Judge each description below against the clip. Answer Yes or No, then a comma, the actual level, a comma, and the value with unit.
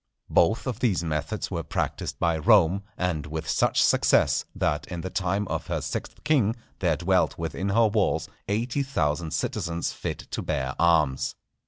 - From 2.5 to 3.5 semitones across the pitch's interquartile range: No, average, 4.4 semitones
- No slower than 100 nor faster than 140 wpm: No, average, 165 wpm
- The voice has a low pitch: Yes, very low, 90 Hz